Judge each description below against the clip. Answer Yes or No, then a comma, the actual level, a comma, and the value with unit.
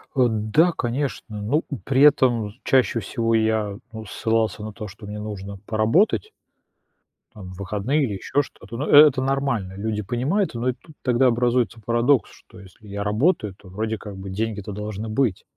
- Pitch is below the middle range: Yes, low, 110 Hz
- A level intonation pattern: No, average, 3.9 semitones